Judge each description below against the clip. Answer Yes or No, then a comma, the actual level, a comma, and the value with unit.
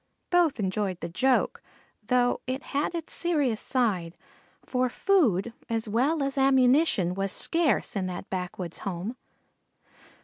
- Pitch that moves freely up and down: Yes, wide, 6.3 semitones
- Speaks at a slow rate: Yes, slow, 130 wpm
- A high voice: Yes, high, 245 Hz